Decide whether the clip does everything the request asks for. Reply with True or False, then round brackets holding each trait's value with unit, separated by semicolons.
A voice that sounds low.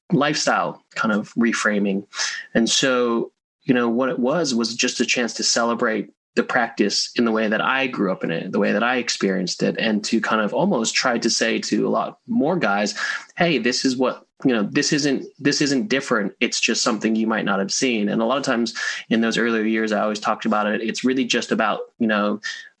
True (115 Hz)